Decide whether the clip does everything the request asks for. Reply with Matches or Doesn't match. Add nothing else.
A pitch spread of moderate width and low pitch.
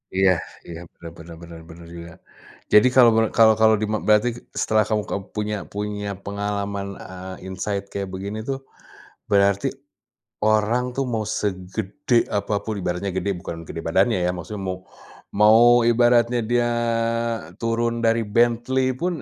Matches